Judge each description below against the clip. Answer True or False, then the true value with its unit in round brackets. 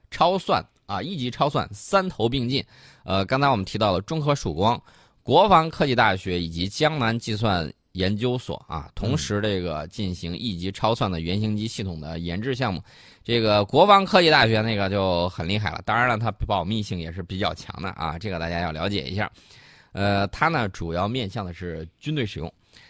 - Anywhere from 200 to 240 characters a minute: False (290 characters per minute)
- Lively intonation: False (5.0 semitones)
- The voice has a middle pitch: False (100 Hz)